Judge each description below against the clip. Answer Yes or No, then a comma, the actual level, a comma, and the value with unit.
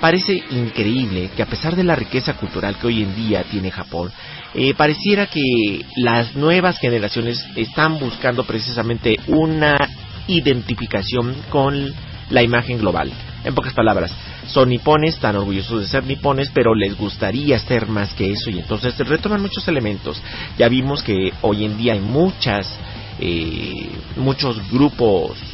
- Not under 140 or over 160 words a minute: Yes, average, 150 wpm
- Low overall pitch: Yes, low, 120 Hz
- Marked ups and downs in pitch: No, average, 4.9 semitones